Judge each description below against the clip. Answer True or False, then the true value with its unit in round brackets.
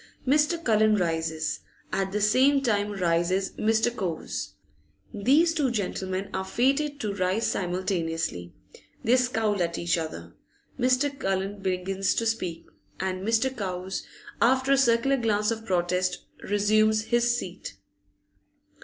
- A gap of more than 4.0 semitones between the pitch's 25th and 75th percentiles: True (4.6 semitones)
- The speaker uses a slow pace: True (125 wpm)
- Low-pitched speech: False (205 Hz)